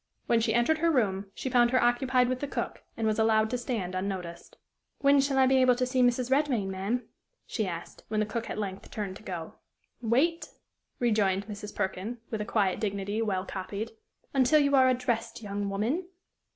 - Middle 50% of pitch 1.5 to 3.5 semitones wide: No, average, 4.2 semitones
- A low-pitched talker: No, high, 225 Hz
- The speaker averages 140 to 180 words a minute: No, average, 195 wpm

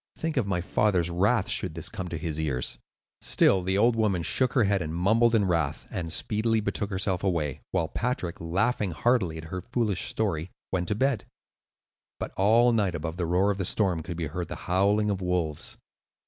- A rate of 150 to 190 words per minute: No, average, 200 wpm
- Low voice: Yes, very low, 95 Hz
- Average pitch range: Yes, average, 4.0 semitones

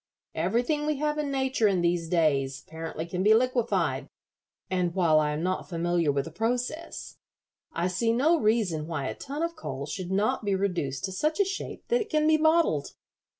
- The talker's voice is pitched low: No, high, 195 Hz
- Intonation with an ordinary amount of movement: No, wide, 9.0 semitones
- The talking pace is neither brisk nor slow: Yes, average, 195 wpm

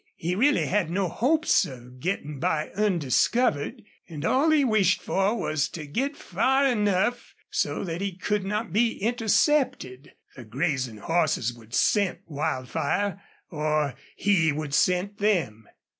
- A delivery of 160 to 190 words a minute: No, average, 140 wpm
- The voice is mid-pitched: Yes, medium, 180 Hz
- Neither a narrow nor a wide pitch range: No, wide, 6.5 semitones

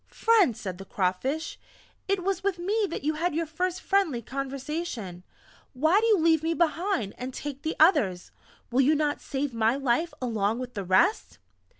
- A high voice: Yes, very high, 295 Hz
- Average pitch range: No, wide, 6.5 semitones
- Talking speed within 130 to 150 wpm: No, average, 180 wpm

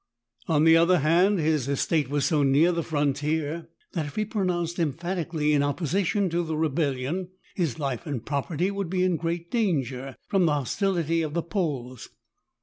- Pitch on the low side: No, medium, 160 Hz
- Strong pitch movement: No, average, 3.4 semitones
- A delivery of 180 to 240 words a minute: Yes, average, 185 wpm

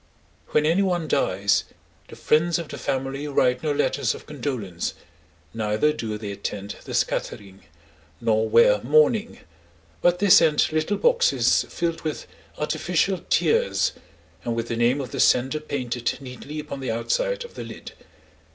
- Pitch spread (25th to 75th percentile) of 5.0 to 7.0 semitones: Yes, wide, 5.6 semitones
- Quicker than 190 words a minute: No, average, 150 wpm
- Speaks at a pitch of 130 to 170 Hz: Yes, medium, 140 Hz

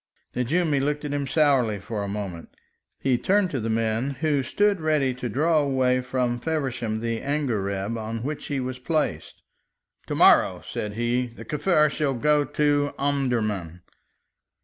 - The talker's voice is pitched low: Yes, low, 130 Hz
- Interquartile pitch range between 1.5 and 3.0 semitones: No, average, 4.5 semitones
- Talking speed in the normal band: Yes, average, 155 wpm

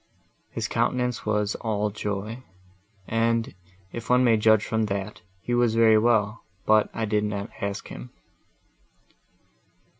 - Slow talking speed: Yes, slow, 130 wpm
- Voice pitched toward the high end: No, low, 110 Hz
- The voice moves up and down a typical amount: No, narrow, 1.8 semitones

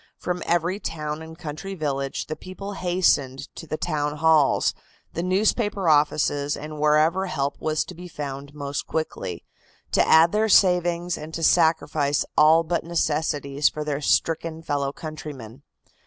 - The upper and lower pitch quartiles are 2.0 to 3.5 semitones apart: Yes, average, 2.9 semitones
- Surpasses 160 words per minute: No, average, 150 wpm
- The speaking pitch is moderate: Yes, medium, 155 Hz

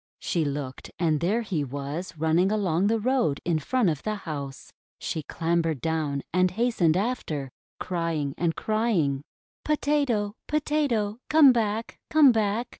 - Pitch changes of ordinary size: No, wide, 6.5 semitones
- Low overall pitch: No, medium, 185 Hz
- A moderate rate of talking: Yes, average, 150 wpm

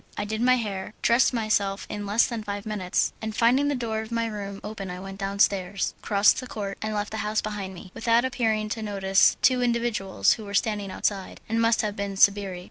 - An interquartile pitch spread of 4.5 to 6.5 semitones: No, narrow, 2.4 semitones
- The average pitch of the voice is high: Yes, high, 210 Hz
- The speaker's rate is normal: No, fast, 215 wpm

